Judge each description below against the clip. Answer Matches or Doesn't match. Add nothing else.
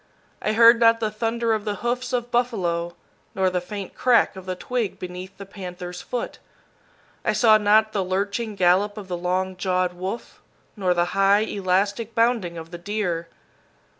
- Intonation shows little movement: Doesn't match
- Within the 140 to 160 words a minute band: Doesn't match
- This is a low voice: Doesn't match